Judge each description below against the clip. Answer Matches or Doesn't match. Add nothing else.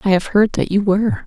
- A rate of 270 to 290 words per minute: Matches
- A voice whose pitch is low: Doesn't match